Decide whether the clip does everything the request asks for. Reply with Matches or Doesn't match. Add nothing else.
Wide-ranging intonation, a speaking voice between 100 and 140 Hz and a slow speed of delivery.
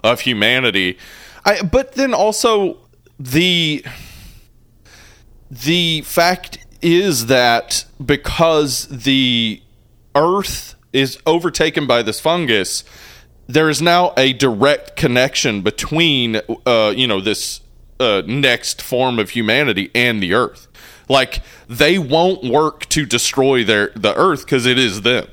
Matches